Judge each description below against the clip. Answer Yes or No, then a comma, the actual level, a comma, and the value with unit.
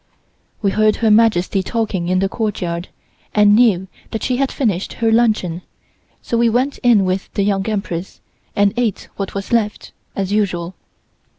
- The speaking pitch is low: No, high, 205 Hz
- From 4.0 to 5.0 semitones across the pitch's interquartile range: No, average, 3.1 semitones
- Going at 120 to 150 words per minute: No, average, 165 wpm